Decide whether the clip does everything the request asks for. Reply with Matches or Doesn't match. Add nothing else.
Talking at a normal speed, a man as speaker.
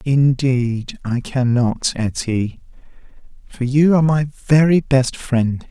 Doesn't match